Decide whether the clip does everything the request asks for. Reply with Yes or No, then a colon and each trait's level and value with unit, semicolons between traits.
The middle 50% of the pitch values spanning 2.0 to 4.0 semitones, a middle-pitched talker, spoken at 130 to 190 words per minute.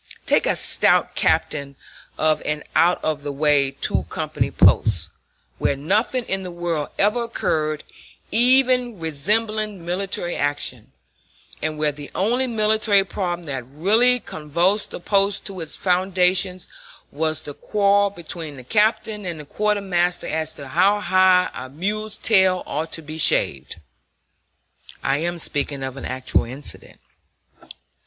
No: average, 5.3 semitones; medium, 175 Hz; average, 140 wpm